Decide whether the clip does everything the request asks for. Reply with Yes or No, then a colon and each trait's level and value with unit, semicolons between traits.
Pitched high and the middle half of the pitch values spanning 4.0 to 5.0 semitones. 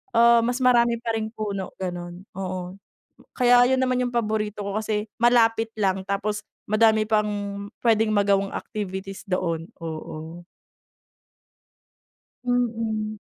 No: high, 215 Hz; average, 3.2 semitones